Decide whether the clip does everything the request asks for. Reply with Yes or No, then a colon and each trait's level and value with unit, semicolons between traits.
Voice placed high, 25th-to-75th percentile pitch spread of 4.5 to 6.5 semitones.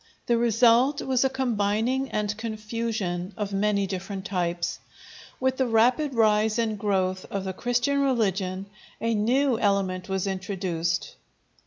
No: high, 210 Hz; average, 3.8 semitones